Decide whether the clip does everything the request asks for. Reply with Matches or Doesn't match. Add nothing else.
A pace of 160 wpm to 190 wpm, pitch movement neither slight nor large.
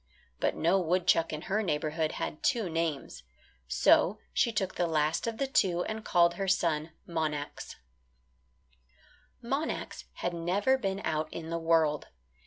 Doesn't match